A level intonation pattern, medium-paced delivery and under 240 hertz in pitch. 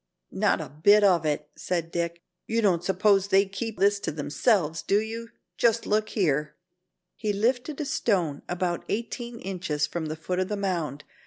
No: average, 4.4 semitones; average, 180 wpm; high, 190 Hz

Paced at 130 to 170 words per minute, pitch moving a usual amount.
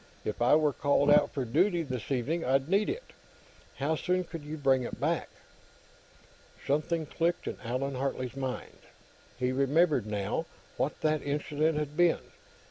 Yes: average, 155 wpm; average, 3.5 semitones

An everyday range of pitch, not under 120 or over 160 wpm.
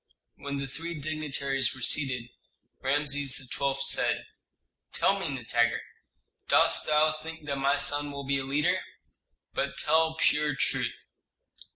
No: narrow, 2.0 semitones; slow, 135 wpm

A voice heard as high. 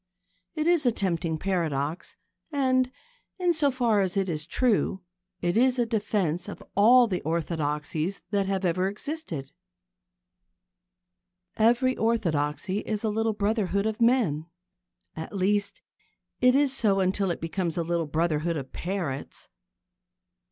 Yes: high, 195 Hz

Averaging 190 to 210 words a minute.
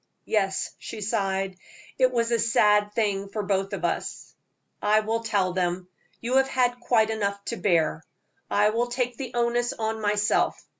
No: average, 165 wpm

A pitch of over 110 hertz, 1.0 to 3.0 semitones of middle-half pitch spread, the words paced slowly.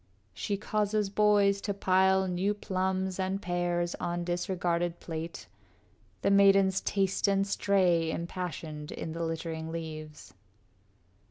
Yes: medium, 185 Hz; average, 2.7 semitones; slow, 115 wpm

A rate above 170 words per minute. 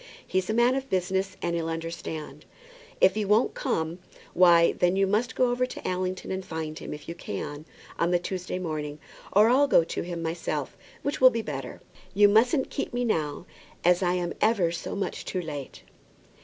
Yes: average, 195 wpm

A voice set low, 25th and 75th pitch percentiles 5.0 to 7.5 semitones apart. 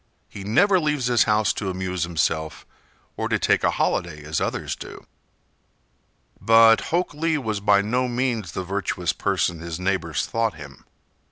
Yes: low, 100 Hz; wide, 5.4 semitones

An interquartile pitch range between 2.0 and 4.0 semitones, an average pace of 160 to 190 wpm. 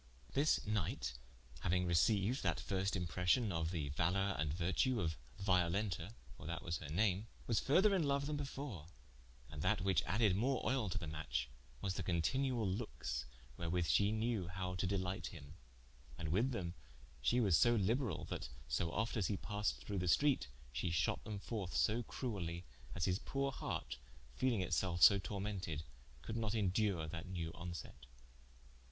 No: average, 4.6 semitones; average, 170 wpm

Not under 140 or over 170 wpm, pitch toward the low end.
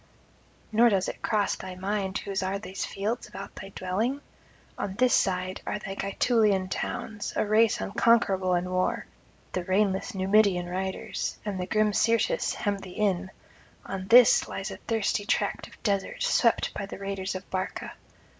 No: average, 165 wpm; high, 195 Hz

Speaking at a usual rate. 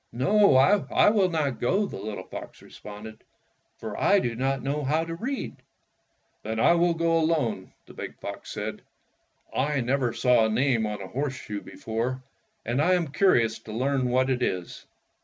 Yes: average, 175 wpm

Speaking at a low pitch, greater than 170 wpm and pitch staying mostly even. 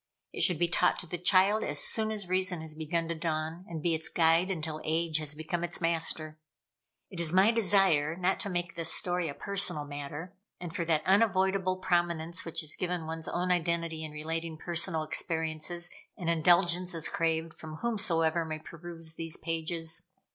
No: medium, 170 Hz; average, 185 wpm; narrow, 2.1 semitones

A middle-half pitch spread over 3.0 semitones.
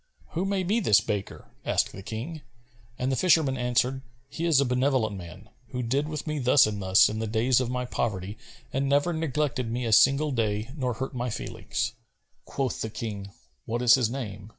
Yes: average, 4.1 semitones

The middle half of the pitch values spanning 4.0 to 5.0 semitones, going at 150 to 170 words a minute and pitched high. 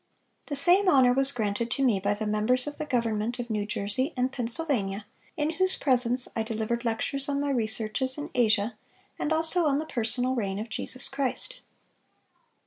No: average, 4.3 semitones; average, 180 wpm; high, 245 Hz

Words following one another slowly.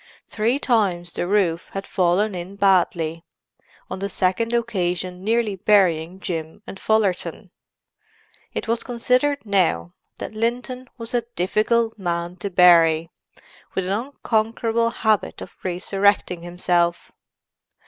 Yes: slow, 120 wpm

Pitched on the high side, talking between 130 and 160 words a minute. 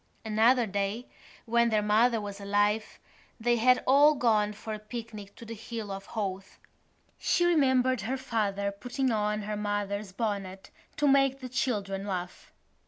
Yes: high, 215 Hz; average, 155 wpm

